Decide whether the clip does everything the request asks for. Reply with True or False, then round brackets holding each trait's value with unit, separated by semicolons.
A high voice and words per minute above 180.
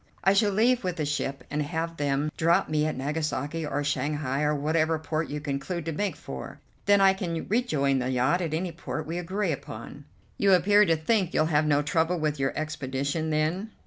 False (155 Hz; 205 wpm)